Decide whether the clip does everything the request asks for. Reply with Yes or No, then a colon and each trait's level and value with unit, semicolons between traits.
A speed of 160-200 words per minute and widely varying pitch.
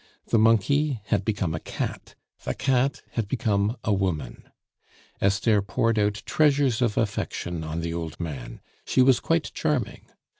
No: average, 150 wpm; wide, 6.2 semitones